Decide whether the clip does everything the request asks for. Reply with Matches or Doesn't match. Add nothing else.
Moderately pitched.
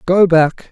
Matches